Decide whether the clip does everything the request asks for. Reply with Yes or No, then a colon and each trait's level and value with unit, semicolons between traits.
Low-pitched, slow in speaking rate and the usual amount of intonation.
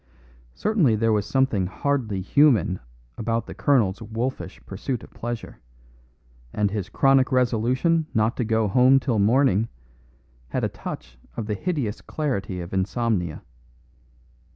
Yes: low, 115 Hz; slow, 130 wpm; average, 4.5 semitones